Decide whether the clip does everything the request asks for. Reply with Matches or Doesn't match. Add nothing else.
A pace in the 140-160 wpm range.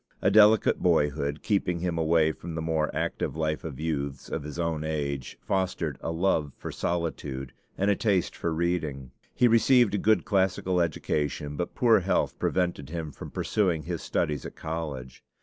Doesn't match